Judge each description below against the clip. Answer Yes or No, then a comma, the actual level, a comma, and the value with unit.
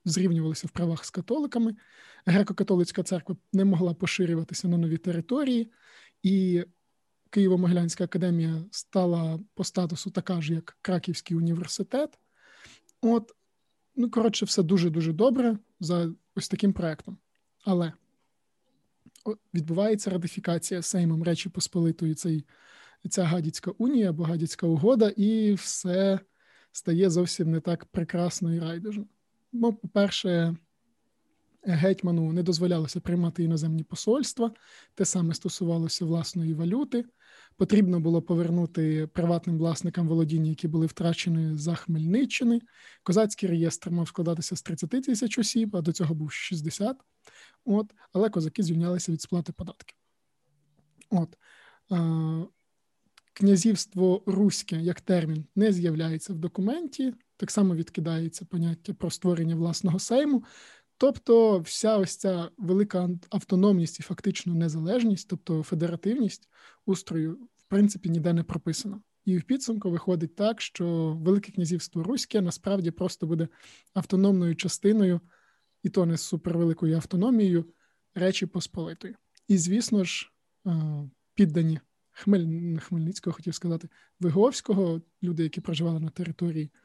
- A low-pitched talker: No, medium, 180 Hz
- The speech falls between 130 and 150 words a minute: No, average, 115 wpm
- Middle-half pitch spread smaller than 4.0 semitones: Yes, average, 3.2 semitones